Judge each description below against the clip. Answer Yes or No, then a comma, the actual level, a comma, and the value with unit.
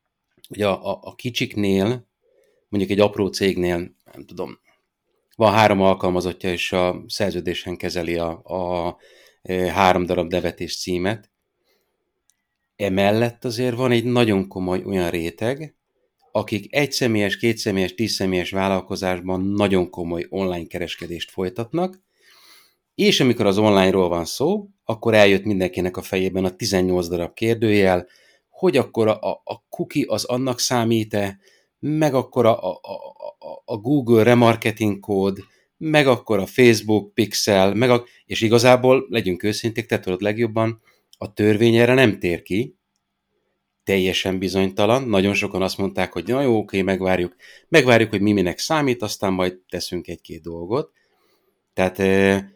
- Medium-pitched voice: No, low, 100 Hz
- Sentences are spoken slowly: No, average, 135 wpm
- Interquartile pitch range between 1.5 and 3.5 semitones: No, average, 4.3 semitones